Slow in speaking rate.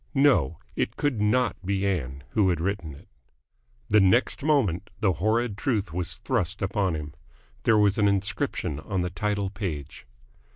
No: average, 160 wpm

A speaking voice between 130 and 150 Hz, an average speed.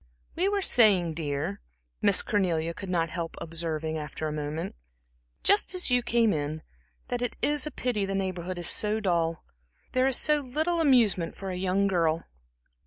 No: medium, 185 Hz; average, 175 wpm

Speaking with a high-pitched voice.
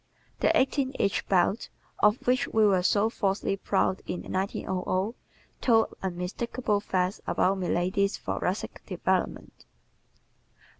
Yes: high, 200 Hz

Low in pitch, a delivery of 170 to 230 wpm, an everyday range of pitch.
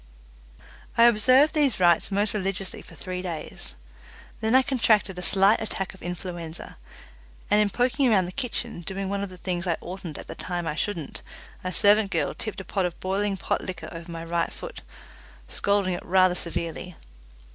No: high, 190 Hz; average, 180 wpm; average, 3.1 semitones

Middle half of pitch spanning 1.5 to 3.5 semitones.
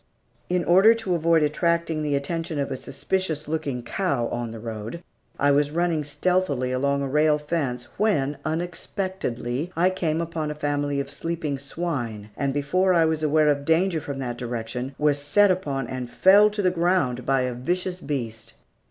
No: average, 4.3 semitones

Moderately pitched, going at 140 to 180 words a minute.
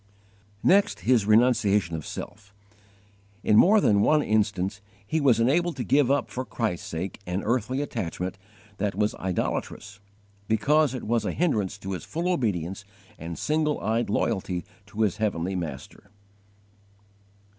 No: low, 110 Hz; average, 145 wpm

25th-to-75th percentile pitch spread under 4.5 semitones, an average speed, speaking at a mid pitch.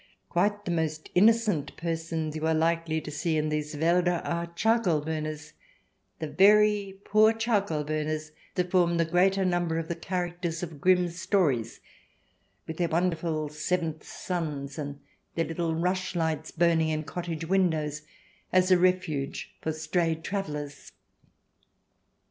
Yes: narrow, 2.6 semitones; average, 145 wpm; medium, 165 Hz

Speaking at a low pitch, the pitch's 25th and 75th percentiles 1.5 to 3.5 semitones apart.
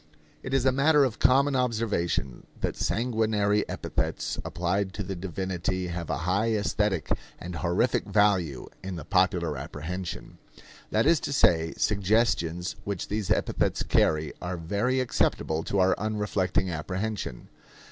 No: very low, 95 Hz; average, 4.0 semitones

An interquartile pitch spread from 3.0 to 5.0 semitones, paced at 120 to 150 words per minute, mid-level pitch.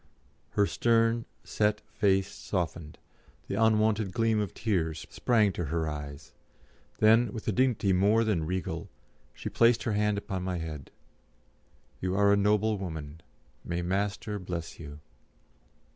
No: average, 4.0 semitones; average, 140 wpm; low, 100 Hz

